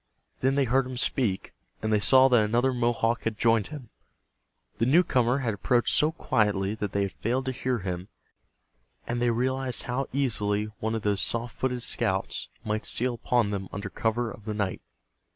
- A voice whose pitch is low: Yes, low, 115 Hz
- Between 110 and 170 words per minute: No, average, 185 wpm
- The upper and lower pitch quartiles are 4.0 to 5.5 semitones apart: No, average, 3.3 semitones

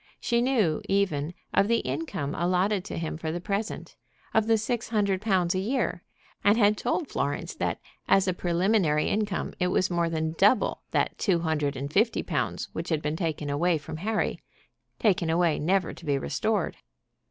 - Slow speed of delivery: No, average, 180 wpm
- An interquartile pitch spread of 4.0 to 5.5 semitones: Yes, average, 4.7 semitones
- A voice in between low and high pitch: Yes, medium, 180 Hz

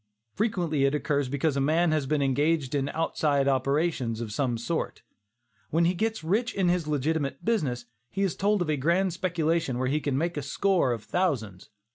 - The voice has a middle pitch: Yes, medium, 150 Hz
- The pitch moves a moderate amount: Yes, average, 4.2 semitones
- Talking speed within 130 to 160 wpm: No, average, 190 wpm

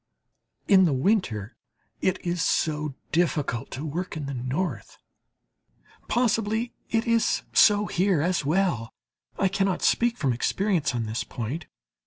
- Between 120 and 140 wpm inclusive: Yes, slow, 135 wpm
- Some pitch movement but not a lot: No, wide, 6.5 semitones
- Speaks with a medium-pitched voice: Yes, medium, 175 Hz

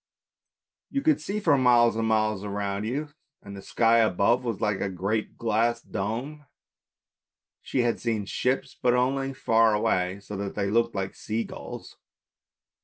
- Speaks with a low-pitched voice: Yes, low, 115 Hz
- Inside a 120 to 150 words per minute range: No, average, 160 wpm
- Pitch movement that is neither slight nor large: Yes, average, 3.5 semitones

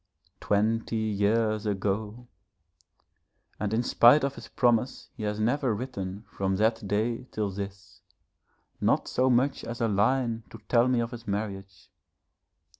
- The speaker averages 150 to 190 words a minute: No, average, 140 wpm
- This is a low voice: Yes, low, 110 Hz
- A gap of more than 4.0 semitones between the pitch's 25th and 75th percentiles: No, average, 2.8 semitones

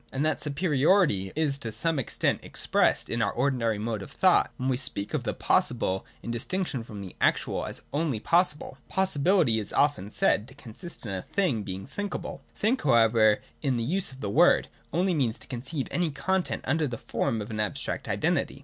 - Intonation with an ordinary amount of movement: No, wide, 6.5 semitones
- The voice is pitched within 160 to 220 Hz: No, low, 135 Hz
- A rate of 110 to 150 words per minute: No, average, 195 wpm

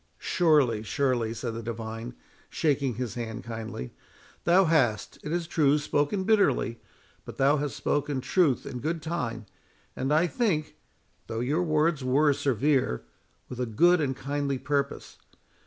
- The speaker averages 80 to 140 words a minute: Yes, slow, 135 wpm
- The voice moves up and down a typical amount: Yes, average, 4.6 semitones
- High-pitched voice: No, medium, 140 Hz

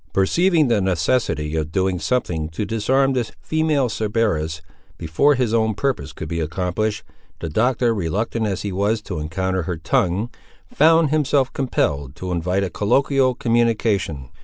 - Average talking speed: Yes, average, 150 wpm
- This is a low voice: Yes, low, 105 Hz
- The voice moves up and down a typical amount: No, wide, 7.0 semitones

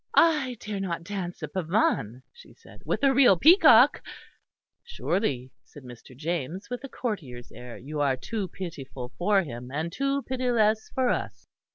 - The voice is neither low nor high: Yes, medium, 180 Hz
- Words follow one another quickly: No, average, 160 wpm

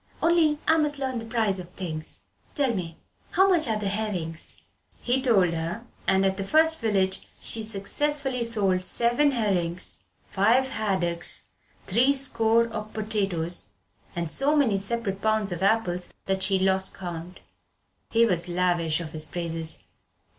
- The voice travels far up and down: No, average, 4.8 semitones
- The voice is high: Yes, high, 200 Hz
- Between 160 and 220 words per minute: No, average, 150 wpm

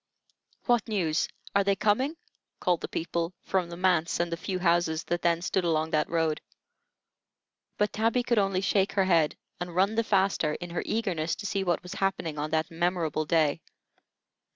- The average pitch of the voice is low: No, medium, 175 Hz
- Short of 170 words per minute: No, average, 180 wpm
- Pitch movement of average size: Yes, average, 3.1 semitones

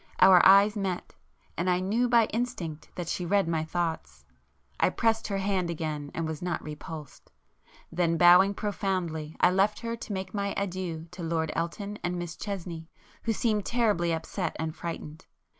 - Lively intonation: No, average, 3.5 semitones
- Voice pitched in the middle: Yes, medium, 180 Hz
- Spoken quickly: No, average, 165 wpm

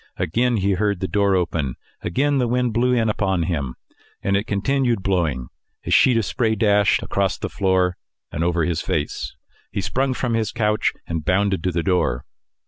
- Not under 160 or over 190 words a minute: Yes, average, 185 wpm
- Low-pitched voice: Yes, low, 100 Hz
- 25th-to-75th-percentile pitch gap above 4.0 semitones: Yes, average, 4.5 semitones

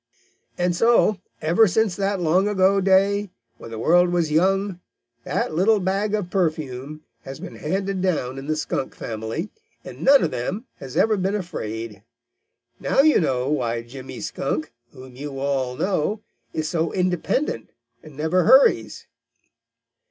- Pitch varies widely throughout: Yes, wide, 6.4 semitones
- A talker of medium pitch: Yes, medium, 175 Hz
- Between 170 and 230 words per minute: No, average, 150 wpm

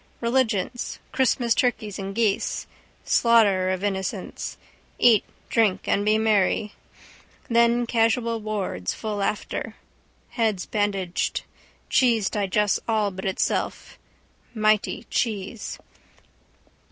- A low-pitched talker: No, high, 215 Hz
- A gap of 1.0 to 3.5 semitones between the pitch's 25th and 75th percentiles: Yes, average, 2.8 semitones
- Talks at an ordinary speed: No, slow, 95 wpm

